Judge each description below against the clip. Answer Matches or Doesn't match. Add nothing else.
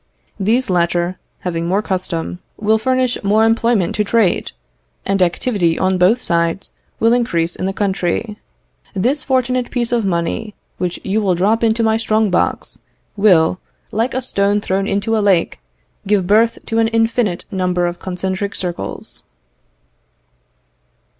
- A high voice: Matches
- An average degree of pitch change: Matches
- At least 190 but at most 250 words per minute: Doesn't match